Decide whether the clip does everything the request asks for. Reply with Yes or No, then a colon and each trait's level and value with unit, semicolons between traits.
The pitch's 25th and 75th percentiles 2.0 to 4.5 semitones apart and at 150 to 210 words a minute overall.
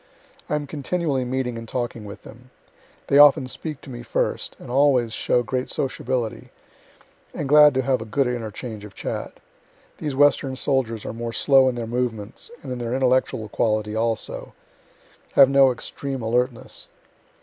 Yes: average, 2.8 semitones; average, 160 wpm